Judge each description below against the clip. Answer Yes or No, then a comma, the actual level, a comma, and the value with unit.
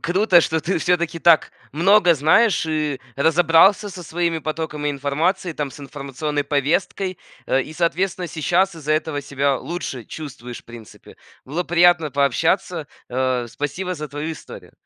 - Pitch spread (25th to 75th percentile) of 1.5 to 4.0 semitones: Yes, average, 3.7 semitones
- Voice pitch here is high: No, medium, 155 Hz